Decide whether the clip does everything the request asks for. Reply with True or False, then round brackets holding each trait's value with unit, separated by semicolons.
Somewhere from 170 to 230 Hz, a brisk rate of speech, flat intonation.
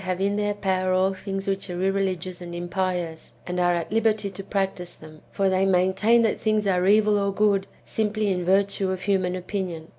True (190 Hz; 210 wpm; 1.8 semitones)